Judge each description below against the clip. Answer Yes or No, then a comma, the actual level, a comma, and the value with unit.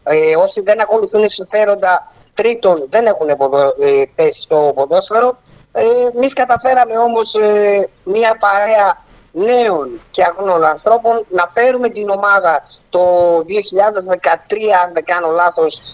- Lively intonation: No, average, 4.7 semitones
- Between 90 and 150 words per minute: Yes, slow, 115 wpm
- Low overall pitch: No, high, 205 Hz